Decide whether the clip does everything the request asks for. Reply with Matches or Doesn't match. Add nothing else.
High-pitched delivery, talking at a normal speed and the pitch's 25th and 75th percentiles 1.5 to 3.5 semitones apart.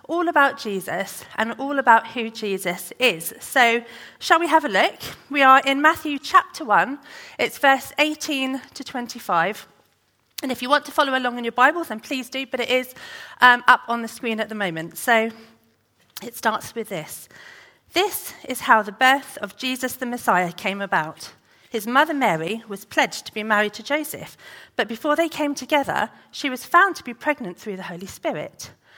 Doesn't match